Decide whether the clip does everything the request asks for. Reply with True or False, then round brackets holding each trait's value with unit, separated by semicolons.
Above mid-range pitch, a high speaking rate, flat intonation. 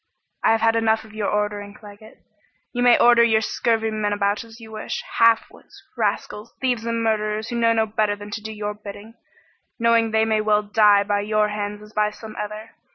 True (215 Hz; 210 wpm; 1.3 semitones)